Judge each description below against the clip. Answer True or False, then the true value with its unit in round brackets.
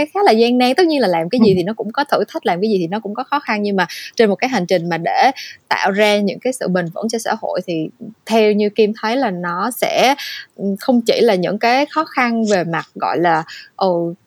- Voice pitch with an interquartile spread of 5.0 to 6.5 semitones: True (5.3 semitones)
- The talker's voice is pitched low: False (215 Hz)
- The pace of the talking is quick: True (275 wpm)